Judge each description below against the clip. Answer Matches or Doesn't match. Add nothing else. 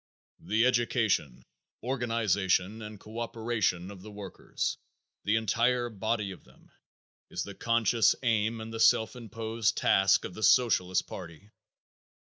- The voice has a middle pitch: Doesn't match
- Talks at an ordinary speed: Doesn't match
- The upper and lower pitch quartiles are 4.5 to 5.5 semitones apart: Doesn't match